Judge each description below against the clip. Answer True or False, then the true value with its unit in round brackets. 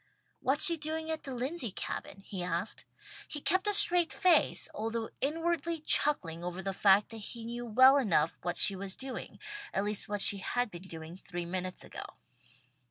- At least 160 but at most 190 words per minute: True (180 wpm)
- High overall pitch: True (225 Hz)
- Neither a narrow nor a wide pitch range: False (8.0 semitones)